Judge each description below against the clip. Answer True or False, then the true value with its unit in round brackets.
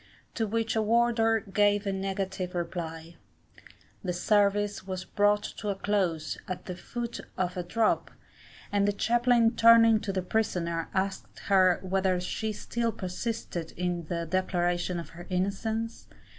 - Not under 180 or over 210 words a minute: False (145 wpm)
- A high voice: True (195 Hz)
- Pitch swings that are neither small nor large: True (3.5 semitones)